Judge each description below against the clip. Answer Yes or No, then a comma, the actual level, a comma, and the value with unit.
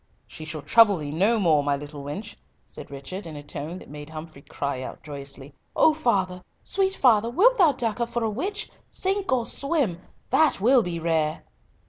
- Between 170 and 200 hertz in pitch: Yes, medium, 185 Hz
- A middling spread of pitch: No, wide, 8.5 semitones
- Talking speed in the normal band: Yes, average, 190 wpm